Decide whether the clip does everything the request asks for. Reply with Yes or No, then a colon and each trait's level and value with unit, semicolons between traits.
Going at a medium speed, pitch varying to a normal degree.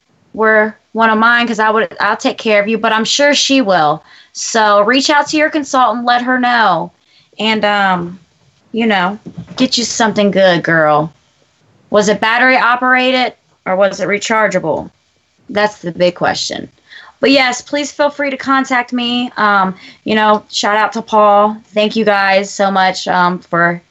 Yes: average, 175 wpm; average, 4.2 semitones